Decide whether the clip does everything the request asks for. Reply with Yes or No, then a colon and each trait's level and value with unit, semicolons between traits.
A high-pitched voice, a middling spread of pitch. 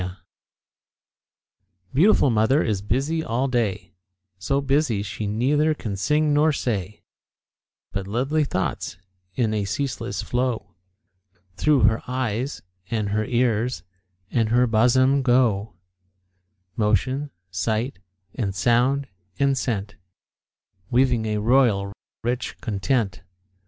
No: low, 120 Hz; average, 4.2 semitones